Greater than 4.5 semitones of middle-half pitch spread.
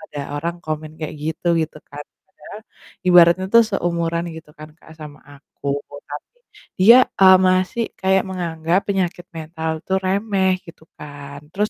No: average, 3.4 semitones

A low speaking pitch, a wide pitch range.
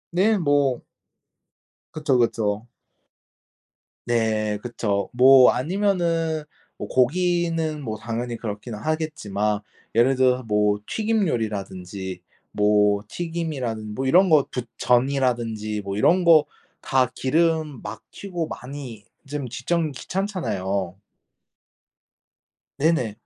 Yes: low, 125 Hz; wide, 7.0 semitones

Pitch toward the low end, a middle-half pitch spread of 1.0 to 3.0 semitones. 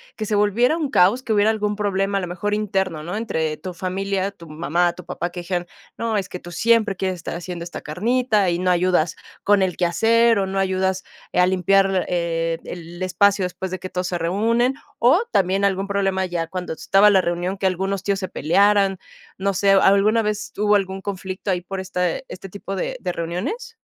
No: high, 190 Hz; narrow, 2.4 semitones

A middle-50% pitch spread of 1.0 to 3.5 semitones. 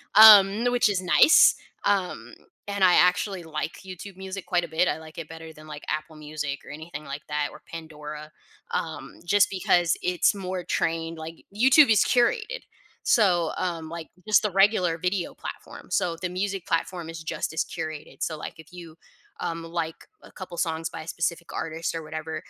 Yes: average, 3.1 semitones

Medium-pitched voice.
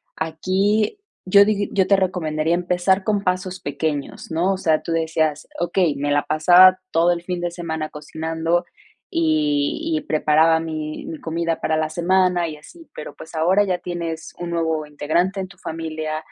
Yes: medium, 170 Hz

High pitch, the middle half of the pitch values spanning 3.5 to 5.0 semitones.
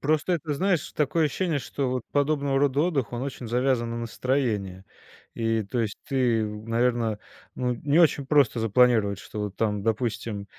No: low, 125 Hz; average, 4.1 semitones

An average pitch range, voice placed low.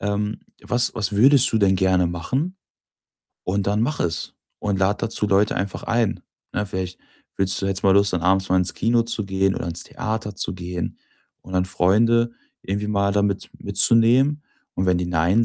Yes: average, 3.3 semitones; low, 100 Hz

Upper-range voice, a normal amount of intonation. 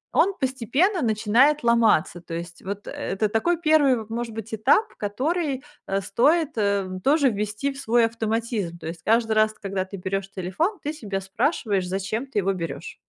No: high, 225 Hz; wide, 5.7 semitones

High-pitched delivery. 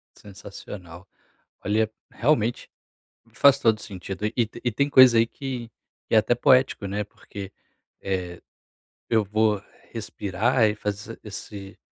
No: low, 105 Hz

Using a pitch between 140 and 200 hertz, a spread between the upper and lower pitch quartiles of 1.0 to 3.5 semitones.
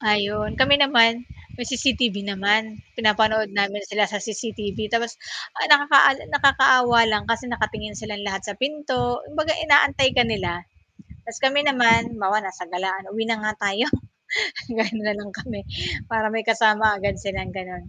No: high, 220 Hz; average, 3.1 semitones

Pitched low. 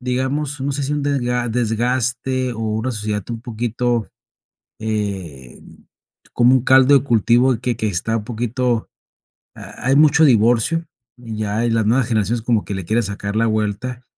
Yes: low, 120 Hz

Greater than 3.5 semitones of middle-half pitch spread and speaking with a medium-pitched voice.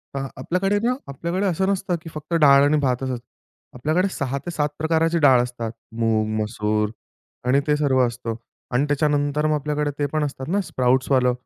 Yes: average, 4.0 semitones; medium, 145 Hz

